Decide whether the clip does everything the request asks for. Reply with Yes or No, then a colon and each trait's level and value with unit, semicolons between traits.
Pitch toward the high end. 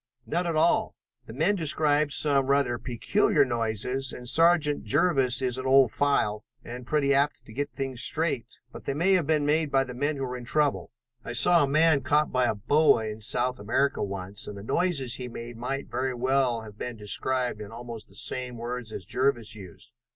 No: low, 130 Hz